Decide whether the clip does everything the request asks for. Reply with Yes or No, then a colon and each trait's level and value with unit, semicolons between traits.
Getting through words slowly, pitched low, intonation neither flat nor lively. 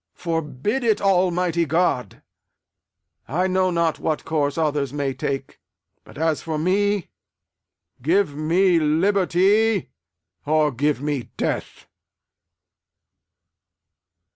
No: slow, 95 wpm; medium, 165 Hz; average, 3.9 semitones